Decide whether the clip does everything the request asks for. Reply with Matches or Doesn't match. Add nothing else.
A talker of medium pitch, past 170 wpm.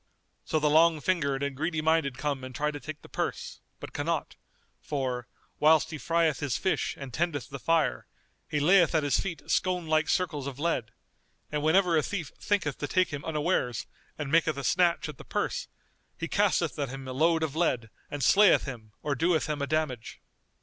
Matches